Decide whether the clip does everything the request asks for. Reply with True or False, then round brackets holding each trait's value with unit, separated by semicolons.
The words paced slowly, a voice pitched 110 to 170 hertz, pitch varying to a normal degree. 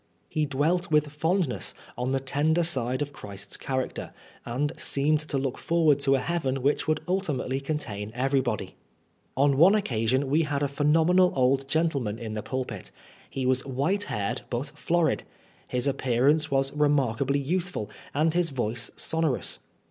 False (160 wpm; 140 Hz; 3.3 semitones)